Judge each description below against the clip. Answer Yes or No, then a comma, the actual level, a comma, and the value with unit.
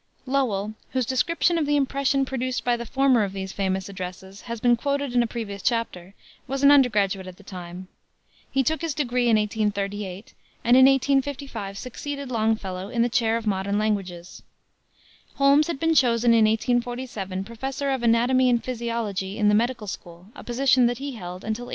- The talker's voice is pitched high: Yes, high, 235 Hz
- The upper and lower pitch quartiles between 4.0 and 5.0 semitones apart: Yes, average, 4.6 semitones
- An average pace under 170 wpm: No, average, 180 wpm